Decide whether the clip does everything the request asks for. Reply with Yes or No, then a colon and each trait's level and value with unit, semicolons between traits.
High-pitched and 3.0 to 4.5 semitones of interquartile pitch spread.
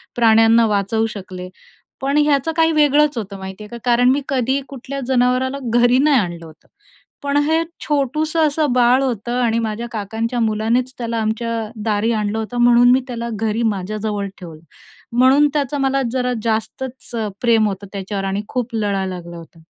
Yes: high, 235 Hz; average, 3.8 semitones